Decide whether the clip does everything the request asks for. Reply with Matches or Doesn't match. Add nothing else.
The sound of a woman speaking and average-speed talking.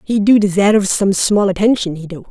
Doesn't match